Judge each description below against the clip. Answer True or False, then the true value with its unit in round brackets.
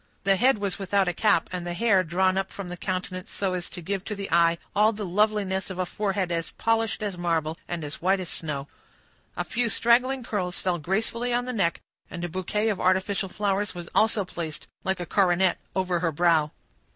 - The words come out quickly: True (210 wpm)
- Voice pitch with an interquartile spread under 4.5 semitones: True (2.9 semitones)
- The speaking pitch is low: False (190 Hz)